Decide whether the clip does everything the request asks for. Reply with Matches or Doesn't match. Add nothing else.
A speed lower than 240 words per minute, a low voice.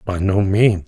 Matches